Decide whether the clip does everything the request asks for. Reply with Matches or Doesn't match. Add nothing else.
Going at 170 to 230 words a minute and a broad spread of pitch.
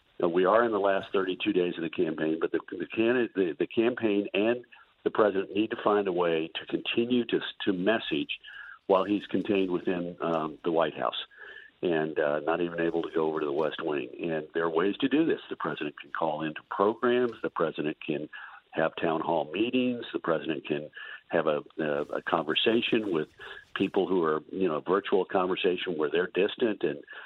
Matches